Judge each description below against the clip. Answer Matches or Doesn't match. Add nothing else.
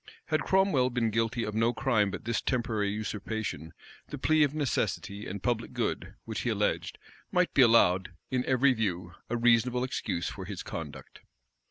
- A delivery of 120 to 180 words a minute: Matches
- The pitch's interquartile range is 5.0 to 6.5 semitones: Doesn't match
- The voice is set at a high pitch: Doesn't match